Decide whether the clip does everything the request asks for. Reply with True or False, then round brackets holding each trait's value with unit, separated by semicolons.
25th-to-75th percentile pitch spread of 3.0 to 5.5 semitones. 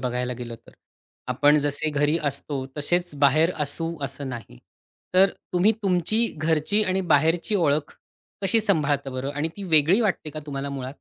True (4.1 semitones)